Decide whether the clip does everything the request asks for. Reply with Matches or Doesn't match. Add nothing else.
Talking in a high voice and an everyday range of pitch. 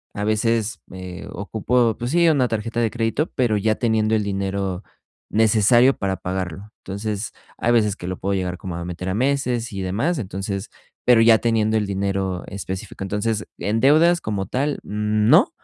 Doesn't match